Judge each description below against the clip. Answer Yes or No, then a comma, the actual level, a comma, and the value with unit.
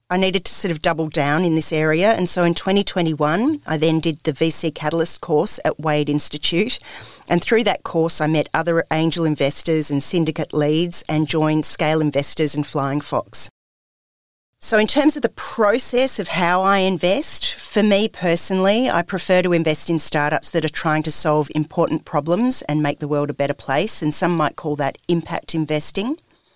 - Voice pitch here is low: No, medium, 160 Hz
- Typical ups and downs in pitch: Yes, average, 3.0 semitones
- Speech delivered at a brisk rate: No, average, 190 wpm